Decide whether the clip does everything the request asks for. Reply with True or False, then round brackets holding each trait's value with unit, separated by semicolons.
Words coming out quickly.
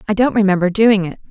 True (230 wpm)